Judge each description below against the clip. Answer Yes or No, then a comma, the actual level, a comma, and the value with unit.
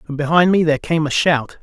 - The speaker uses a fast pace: Yes, fast, 260 wpm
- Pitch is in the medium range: Yes, medium, 155 Hz